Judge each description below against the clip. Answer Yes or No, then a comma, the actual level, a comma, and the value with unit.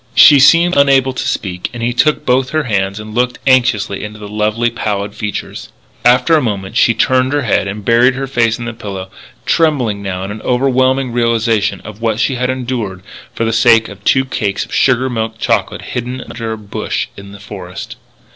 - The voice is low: Yes, low, 115 Hz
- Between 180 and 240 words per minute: Yes, average, 195 wpm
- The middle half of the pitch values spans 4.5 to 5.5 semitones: No, average, 3.7 semitones